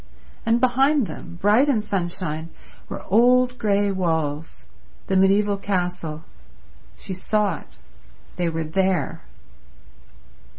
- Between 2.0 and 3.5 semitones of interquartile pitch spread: No, average, 4.6 semitones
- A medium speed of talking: No, slow, 95 wpm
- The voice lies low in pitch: No, high, 190 Hz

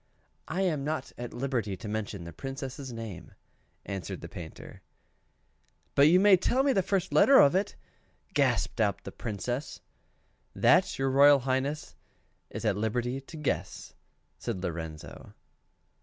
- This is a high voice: No, low, 130 Hz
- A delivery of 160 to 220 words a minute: No, average, 140 wpm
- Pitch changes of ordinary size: No, wide, 6.1 semitones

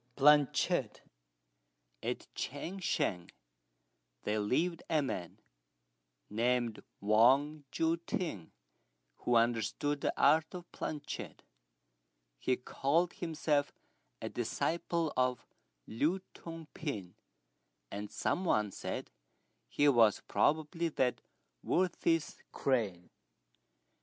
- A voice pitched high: No, medium, 145 Hz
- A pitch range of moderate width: No, wide, 6.0 semitones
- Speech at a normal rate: No, slow, 90 wpm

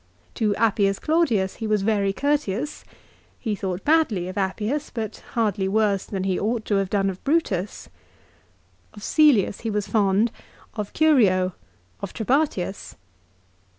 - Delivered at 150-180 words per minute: No, average, 140 wpm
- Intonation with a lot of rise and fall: No, average, 3.4 semitones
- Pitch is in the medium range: No, high, 210 Hz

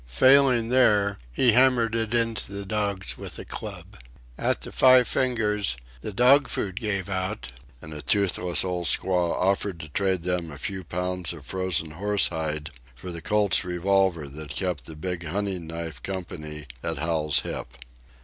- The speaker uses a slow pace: No, average, 165 wpm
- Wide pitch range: No, average, 4.2 semitones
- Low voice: Yes, very low, 95 Hz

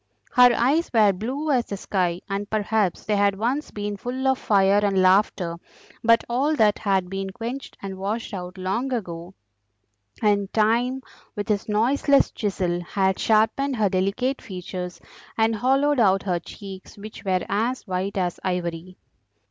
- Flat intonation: No, average, 3.8 semitones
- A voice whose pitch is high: Yes, high, 205 Hz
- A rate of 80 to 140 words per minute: No, average, 155 wpm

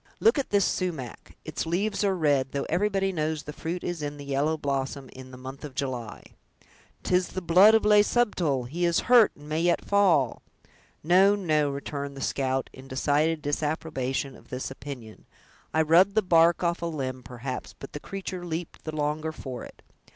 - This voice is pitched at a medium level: Yes, medium, 155 Hz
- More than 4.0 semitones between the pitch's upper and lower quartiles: Yes, average, 4.7 semitones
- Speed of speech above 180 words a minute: Yes, average, 190 wpm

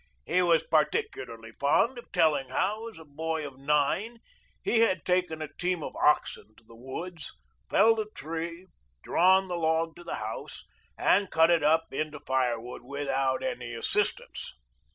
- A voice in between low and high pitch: Yes, medium, 160 Hz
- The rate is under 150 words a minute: No, average, 160 wpm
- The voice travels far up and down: No, average, 4.8 semitones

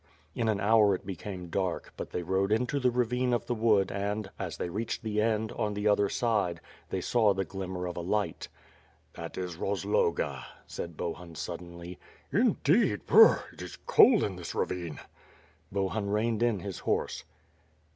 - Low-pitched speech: Yes, low, 100 Hz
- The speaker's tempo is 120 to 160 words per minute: No, average, 170 wpm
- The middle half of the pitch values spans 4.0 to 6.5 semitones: No, average, 3.4 semitones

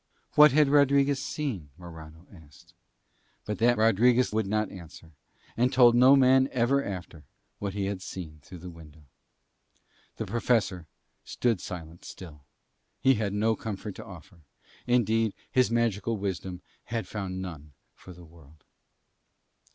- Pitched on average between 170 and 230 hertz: No, low, 100 Hz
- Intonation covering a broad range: Yes, wide, 5.7 semitones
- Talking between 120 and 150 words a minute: Yes, average, 140 wpm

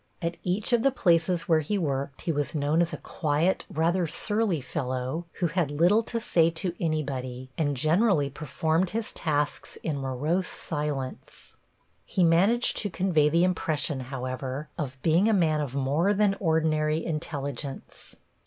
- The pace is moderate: Yes, average, 155 wpm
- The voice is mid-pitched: Yes, medium, 160 Hz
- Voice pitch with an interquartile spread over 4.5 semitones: No, average, 3.7 semitones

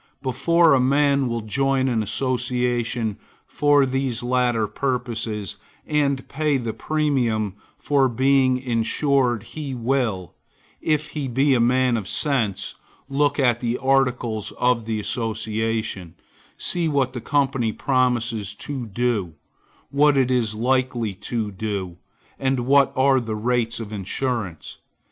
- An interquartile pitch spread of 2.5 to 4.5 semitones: Yes, average, 3.4 semitones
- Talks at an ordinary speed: No, slow, 130 wpm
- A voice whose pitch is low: Yes, low, 125 Hz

